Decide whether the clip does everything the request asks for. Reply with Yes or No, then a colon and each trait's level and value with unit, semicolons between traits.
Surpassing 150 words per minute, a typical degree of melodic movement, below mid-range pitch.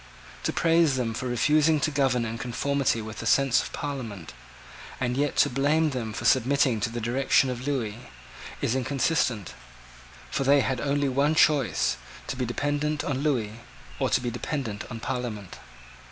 Yes: average, 170 wpm; average, 3.5 semitones; low, 130 Hz